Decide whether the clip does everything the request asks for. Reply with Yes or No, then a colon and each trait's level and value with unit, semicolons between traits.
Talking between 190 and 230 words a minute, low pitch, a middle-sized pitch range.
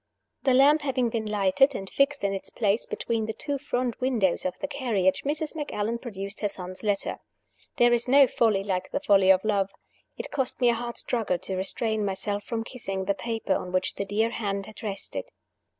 No: average, 200 wpm; high, 220 Hz; average, 4.1 semitones